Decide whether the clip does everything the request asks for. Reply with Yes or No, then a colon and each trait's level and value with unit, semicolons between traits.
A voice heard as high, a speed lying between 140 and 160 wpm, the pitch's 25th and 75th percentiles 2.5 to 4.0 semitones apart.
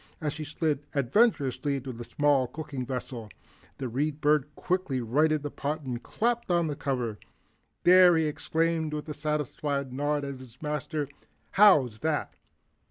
No: medium, 145 Hz; average, 155 wpm; average, 3.0 semitones